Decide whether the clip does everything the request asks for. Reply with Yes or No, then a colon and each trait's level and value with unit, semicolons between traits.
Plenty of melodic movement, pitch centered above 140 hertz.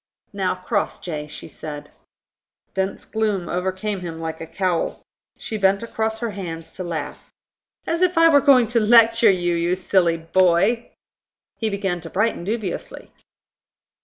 No: average, 4.4 semitones; high, 190 Hz